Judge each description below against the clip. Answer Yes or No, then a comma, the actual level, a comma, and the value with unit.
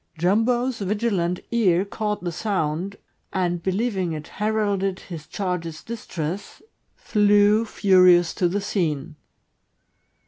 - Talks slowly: Yes, slow, 105 wpm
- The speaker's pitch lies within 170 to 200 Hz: Yes, high, 190 Hz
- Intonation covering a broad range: No, average, 3.2 semitones